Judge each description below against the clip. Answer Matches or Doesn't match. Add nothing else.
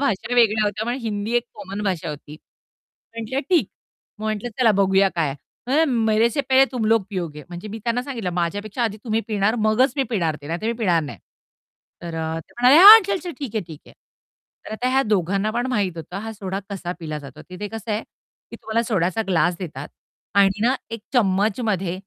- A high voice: Matches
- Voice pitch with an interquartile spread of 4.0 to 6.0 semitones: Matches